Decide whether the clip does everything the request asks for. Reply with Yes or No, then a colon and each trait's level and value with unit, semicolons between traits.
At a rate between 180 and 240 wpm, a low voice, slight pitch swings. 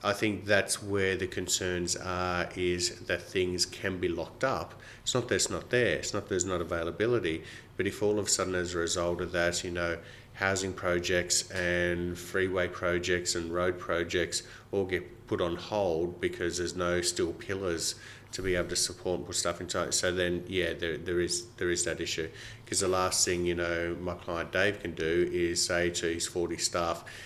Yes: fast, 205 wpm; very low, 90 Hz; narrow, 1.0 semitones